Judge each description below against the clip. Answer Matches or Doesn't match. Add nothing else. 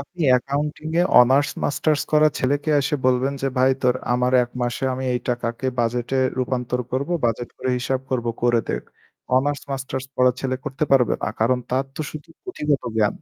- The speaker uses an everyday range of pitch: Doesn't match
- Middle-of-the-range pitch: Doesn't match